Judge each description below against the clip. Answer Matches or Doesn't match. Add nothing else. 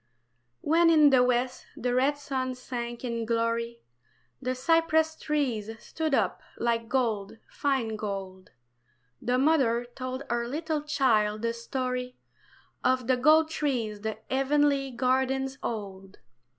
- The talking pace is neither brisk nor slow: Doesn't match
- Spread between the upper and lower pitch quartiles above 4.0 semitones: Doesn't match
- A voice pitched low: Doesn't match